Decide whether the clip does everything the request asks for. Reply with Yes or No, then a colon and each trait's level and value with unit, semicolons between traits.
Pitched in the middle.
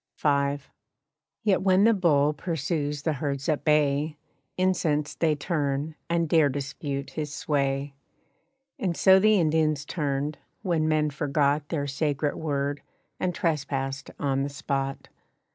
Yes: medium, 150 Hz